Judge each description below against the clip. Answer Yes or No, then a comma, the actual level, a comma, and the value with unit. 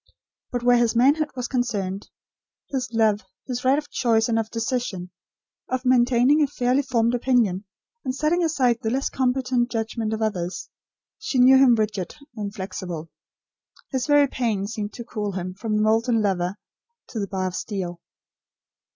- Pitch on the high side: Yes, high, 235 Hz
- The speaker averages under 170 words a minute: Yes, average, 160 wpm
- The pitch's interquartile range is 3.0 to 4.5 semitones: Yes, average, 3.8 semitones